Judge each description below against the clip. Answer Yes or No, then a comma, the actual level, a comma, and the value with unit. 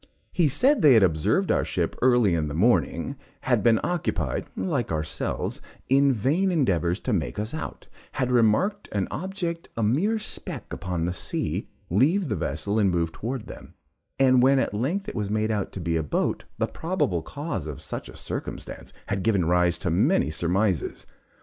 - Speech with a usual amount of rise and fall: No, wide, 8.0 semitones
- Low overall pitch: Yes, low, 110 Hz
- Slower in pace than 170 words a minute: No, average, 180 wpm